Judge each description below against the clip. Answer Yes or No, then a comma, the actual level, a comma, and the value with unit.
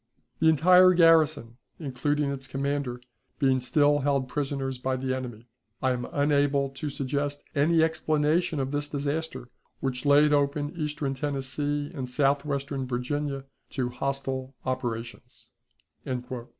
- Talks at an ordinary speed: No, slow, 125 wpm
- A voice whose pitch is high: No, medium, 140 Hz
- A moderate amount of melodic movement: No, narrow, 2.1 semitones